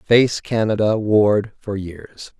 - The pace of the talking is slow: Yes, slow, 125 wpm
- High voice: No, low, 105 Hz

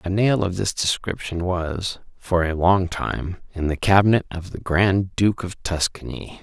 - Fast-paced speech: No, average, 175 wpm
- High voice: No, very low, 90 Hz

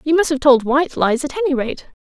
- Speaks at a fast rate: Yes, fast, 265 wpm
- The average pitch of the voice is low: No, very high, 285 Hz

